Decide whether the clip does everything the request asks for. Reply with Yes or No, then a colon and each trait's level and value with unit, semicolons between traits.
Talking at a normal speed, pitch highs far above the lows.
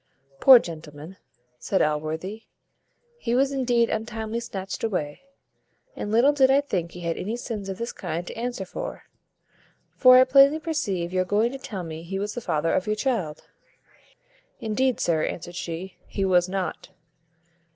Yes: average, 165 wpm; wide, 5.7 semitones